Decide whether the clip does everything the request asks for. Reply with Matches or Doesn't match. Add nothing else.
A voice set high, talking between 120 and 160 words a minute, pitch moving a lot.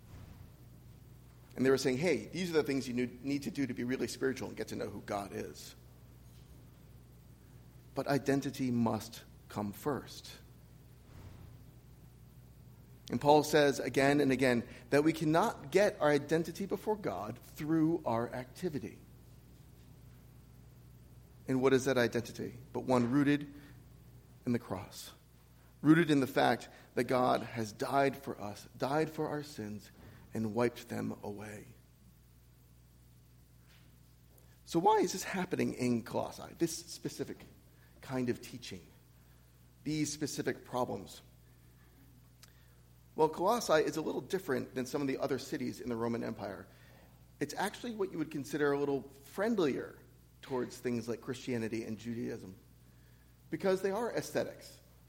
Doesn't match